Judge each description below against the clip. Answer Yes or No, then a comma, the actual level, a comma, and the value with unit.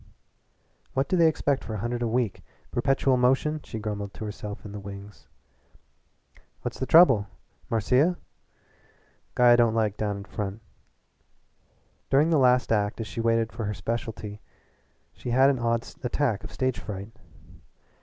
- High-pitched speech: No, low, 115 Hz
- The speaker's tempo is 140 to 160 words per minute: Yes, average, 155 wpm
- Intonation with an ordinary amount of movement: Yes, average, 3.8 semitones